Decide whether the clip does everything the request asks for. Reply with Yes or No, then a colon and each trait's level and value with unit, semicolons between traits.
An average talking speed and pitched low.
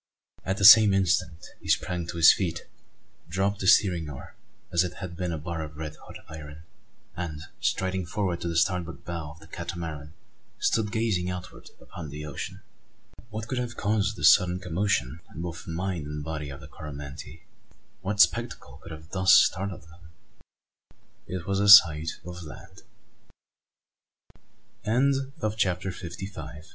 Yes: average, 160 wpm; very low, 85 Hz